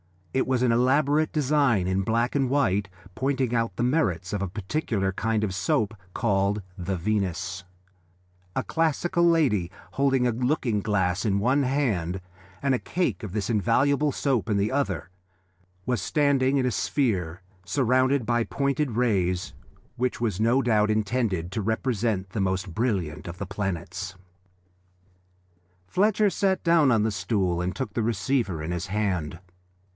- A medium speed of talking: Yes, average, 155 wpm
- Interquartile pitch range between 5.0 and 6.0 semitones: Yes, wide, 5.6 semitones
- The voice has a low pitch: Yes, low, 110 Hz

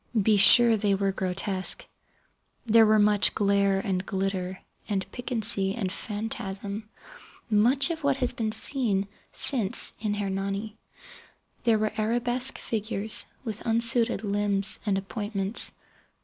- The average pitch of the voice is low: No, high, 210 Hz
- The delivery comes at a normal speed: No, slow, 120 wpm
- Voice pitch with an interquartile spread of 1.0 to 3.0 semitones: Yes, average, 2.7 semitones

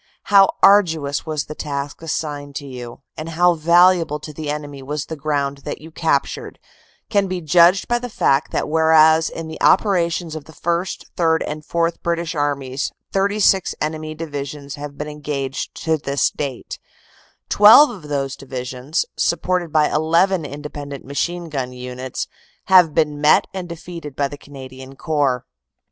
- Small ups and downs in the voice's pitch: No, average, 3.1 semitones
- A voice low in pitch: No, medium, 155 Hz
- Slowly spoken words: No, average, 160 wpm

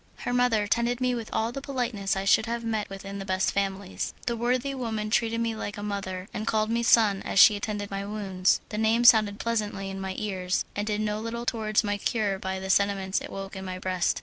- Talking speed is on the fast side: Yes, fast, 240 wpm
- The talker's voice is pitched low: No, high, 210 Hz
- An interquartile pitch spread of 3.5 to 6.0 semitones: No, average, 2.8 semitones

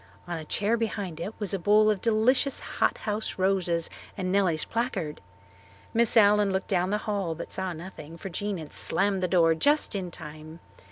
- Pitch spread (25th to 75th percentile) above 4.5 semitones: No, average, 3.7 semitones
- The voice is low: No, high, 195 Hz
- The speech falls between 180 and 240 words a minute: Yes, average, 185 wpm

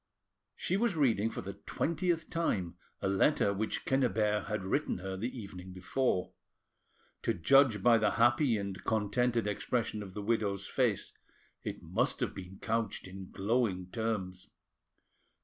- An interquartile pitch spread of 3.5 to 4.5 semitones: Yes, average, 4.0 semitones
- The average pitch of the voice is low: Yes, low, 105 Hz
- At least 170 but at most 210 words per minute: No, average, 145 wpm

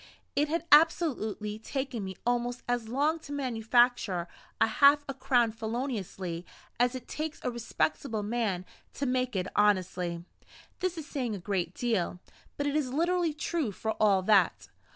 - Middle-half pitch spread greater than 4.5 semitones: Yes, wide, 5.4 semitones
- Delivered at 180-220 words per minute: No, average, 155 wpm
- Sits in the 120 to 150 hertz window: No, high, 240 Hz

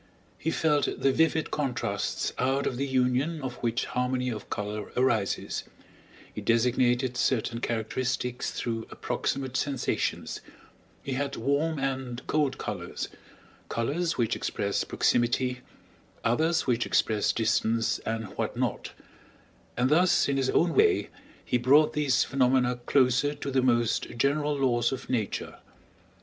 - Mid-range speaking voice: No, low, 125 Hz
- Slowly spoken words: Yes, slow, 130 wpm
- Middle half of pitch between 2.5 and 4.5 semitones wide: Yes, average, 2.8 semitones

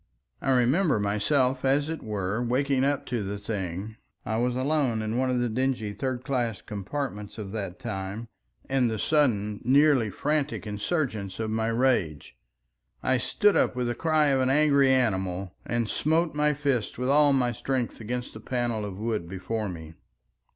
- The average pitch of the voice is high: No, low, 120 Hz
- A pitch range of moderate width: Yes, average, 4.4 semitones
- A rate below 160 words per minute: No, average, 165 wpm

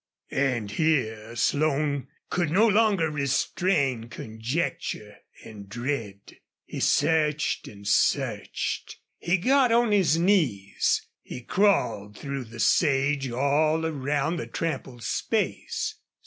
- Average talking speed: No, slow, 105 wpm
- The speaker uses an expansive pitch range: Yes, wide, 5.8 semitones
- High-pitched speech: No, medium, 140 Hz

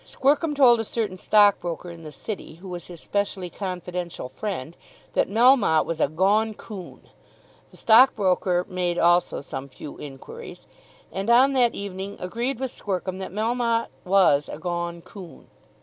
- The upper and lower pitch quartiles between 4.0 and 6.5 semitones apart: Yes, average, 4.5 semitones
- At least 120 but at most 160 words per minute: Yes, average, 150 wpm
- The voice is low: No, high, 190 Hz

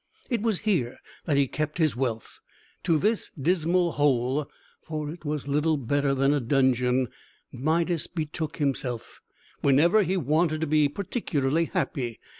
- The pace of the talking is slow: No, average, 145 wpm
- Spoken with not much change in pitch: No, average, 3.7 semitones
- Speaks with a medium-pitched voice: Yes, medium, 150 Hz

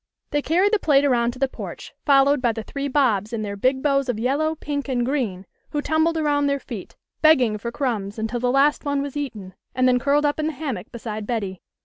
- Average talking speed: No, fast, 240 wpm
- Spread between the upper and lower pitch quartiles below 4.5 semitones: Yes, average, 3.9 semitones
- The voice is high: Yes, very high, 270 Hz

